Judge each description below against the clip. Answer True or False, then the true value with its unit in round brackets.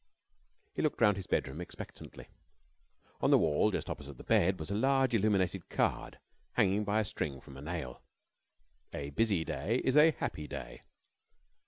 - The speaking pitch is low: True (95 Hz)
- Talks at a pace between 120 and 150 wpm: False (165 wpm)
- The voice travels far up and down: True (6.2 semitones)